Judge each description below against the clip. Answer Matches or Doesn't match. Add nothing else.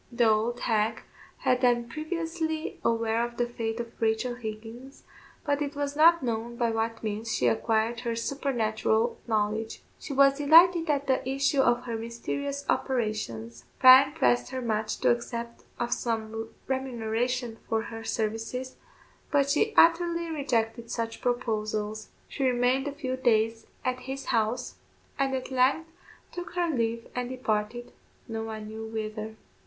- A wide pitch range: Doesn't match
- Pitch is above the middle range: Matches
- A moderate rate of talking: Matches